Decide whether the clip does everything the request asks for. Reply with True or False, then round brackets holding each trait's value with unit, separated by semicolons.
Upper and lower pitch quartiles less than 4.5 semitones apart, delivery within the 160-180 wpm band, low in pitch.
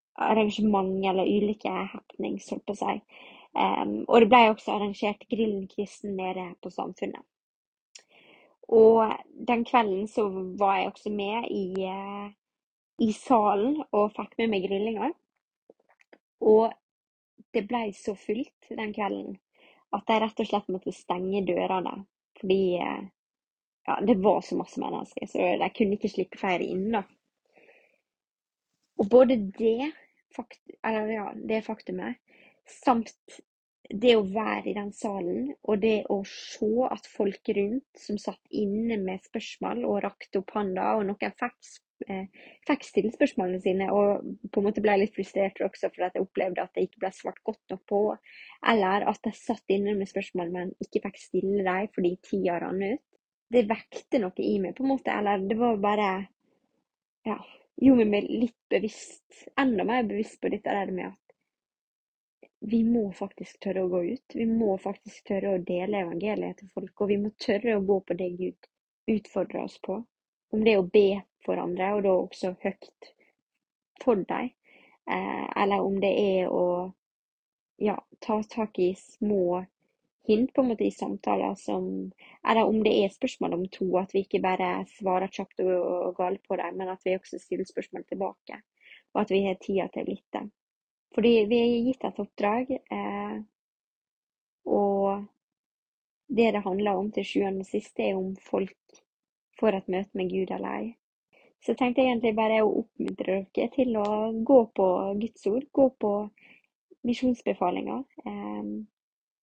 False (3.0 semitones; 165 wpm; 205 Hz)